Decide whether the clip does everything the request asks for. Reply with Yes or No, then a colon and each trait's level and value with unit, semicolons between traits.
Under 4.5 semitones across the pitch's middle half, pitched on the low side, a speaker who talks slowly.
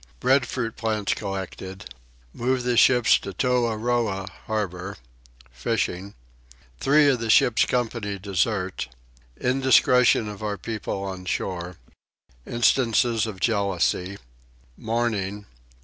Yes: average, 3.7 semitones; low, 110 Hz; slow, 100 wpm